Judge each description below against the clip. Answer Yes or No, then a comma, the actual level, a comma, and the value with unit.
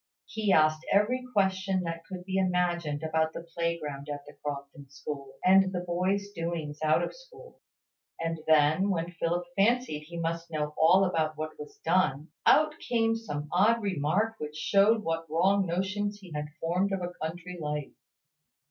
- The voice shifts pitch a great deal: No, average, 3.8 semitones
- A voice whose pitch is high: No, medium, 170 Hz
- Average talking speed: Yes, average, 165 wpm